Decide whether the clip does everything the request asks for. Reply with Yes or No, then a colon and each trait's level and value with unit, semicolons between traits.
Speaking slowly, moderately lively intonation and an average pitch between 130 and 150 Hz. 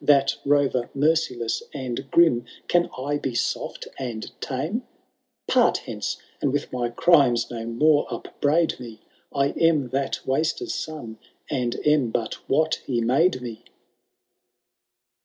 Yes: slow, 130 wpm; average, 4.0 semitones; low, 135 Hz